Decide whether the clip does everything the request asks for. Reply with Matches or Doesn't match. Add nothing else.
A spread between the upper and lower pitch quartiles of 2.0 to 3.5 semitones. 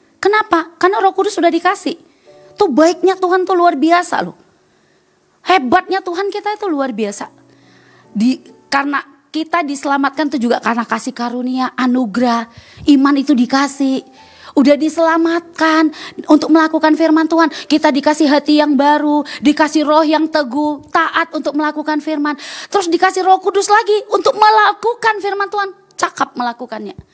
Doesn't match